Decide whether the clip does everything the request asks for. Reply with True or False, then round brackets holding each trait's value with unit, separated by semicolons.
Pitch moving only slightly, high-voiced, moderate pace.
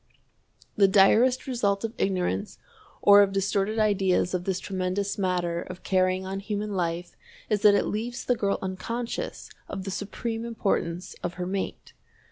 True (2.3 semitones; 195 Hz; 155 wpm)